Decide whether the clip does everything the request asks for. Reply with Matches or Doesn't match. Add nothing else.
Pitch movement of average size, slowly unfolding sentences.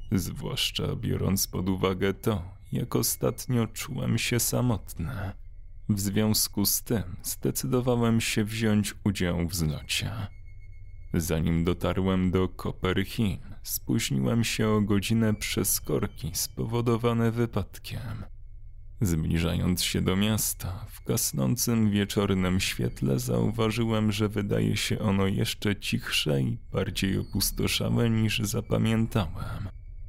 Matches